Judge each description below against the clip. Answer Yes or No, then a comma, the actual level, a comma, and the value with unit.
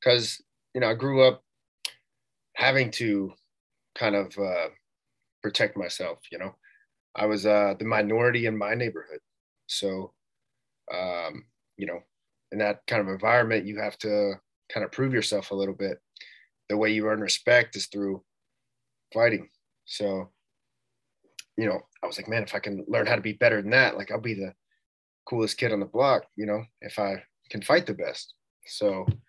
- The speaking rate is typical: Yes, average, 175 wpm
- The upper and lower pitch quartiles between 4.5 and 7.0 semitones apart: No, average, 2.8 semitones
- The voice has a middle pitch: No, low, 105 Hz